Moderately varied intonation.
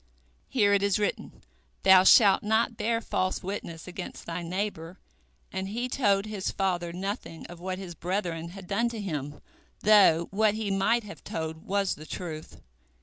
Yes: average, 3.2 semitones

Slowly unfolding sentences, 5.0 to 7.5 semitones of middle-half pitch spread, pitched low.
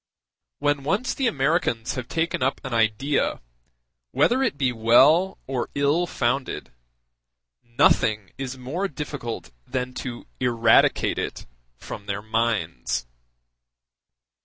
No: slow, 110 wpm; average, 4.2 semitones; low, 130 Hz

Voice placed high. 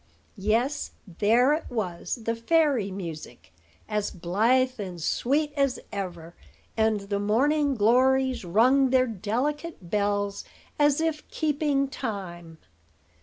Yes: high, 230 Hz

